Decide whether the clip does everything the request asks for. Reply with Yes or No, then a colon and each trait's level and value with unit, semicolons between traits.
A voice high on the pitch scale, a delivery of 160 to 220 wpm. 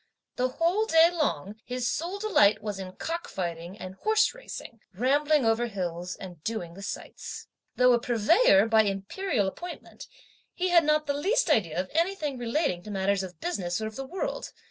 Yes: high, 240 Hz; average, 180 wpm